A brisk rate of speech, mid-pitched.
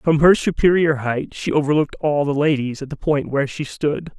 Yes: fast, 215 wpm; medium, 150 Hz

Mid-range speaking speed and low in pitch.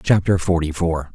Yes: average, 155 wpm; very low, 85 Hz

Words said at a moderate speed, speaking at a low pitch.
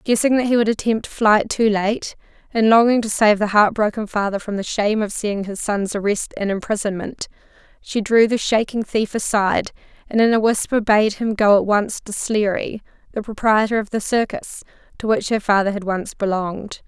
No: average, 190 wpm; high, 210 Hz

